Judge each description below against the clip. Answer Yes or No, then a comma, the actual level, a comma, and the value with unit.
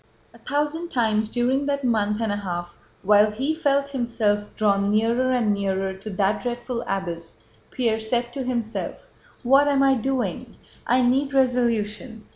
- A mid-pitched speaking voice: No, high, 235 Hz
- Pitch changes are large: No, average, 4.0 semitones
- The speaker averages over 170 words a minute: No, average, 155 wpm